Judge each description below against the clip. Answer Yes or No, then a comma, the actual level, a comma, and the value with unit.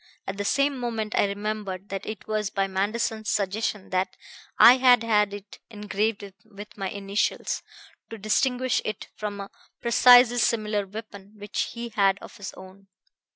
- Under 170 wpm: Yes, average, 155 wpm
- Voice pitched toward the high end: Yes, high, 210 Hz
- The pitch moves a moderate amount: No, narrow, 2.2 semitones